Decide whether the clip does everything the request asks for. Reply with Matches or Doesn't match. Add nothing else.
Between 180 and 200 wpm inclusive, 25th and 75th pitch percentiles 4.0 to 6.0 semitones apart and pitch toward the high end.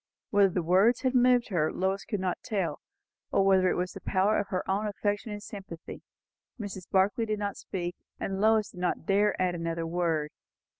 Doesn't match